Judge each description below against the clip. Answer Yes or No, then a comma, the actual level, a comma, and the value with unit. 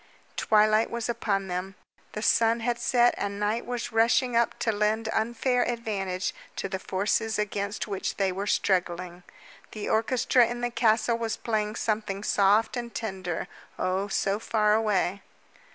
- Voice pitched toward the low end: No, high, 215 Hz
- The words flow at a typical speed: Yes, average, 150 wpm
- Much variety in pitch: No, average, 2.9 semitones